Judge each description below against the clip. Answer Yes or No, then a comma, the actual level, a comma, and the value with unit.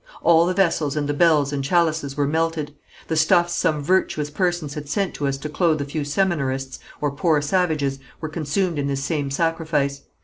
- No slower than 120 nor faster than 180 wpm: No, average, 195 wpm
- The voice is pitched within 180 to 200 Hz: No, medium, 150 Hz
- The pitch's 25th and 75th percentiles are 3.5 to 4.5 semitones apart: No, average, 2.9 semitones